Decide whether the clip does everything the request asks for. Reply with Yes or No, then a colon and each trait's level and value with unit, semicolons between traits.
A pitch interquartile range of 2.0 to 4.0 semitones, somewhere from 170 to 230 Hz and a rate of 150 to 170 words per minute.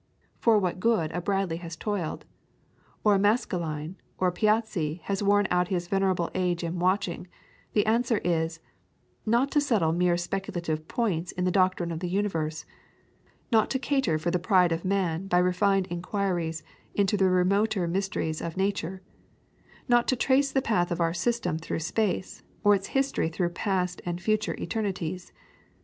Yes: average, 3.2 semitones; medium, 185 Hz; average, 165 wpm